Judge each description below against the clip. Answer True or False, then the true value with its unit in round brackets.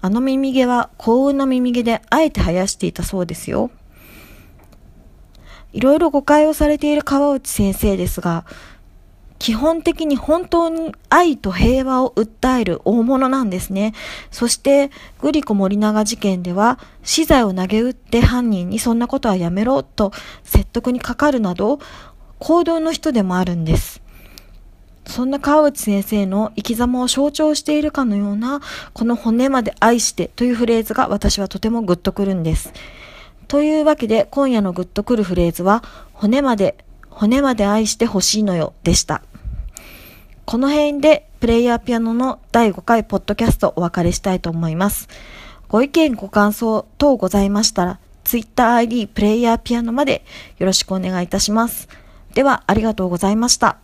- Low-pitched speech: False (225 Hz)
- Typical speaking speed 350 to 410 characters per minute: False (335 characters per minute)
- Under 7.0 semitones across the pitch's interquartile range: True (5.5 semitones)